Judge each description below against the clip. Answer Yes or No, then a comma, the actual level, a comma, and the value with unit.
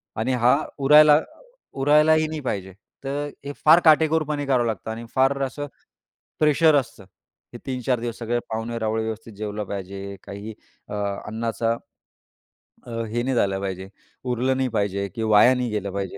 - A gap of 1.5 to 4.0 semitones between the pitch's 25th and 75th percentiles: No, average, 4.5 semitones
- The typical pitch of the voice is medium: No, low, 120 Hz